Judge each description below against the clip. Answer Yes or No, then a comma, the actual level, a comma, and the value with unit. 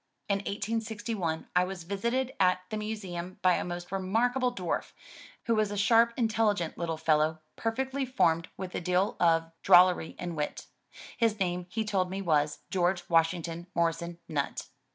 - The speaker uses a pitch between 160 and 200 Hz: Yes, medium, 185 Hz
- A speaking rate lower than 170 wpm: Yes, average, 155 wpm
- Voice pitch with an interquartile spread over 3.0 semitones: Yes, average, 4.1 semitones